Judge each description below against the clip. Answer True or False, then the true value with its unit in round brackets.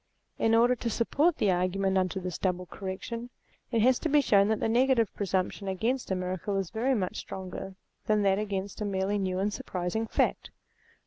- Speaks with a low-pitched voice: False (200 Hz)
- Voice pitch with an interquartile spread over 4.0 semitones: False (3.3 semitones)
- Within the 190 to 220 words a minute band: True (195 wpm)